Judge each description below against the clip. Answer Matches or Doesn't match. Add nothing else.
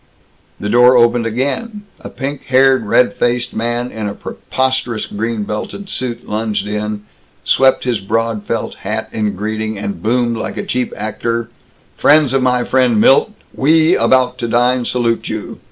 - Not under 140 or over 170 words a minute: Matches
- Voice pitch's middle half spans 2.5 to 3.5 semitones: Matches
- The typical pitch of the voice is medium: Doesn't match